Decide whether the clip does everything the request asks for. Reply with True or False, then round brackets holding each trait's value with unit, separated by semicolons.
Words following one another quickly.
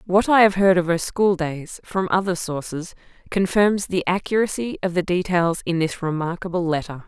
False (180 wpm)